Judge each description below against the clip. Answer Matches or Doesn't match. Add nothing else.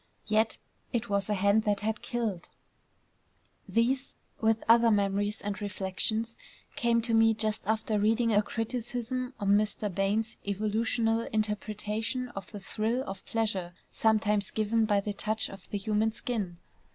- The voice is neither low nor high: Doesn't match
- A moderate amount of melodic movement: Doesn't match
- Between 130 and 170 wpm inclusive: Matches